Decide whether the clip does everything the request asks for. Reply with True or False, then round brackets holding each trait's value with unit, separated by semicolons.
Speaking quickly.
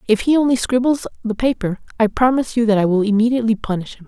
True (220 wpm)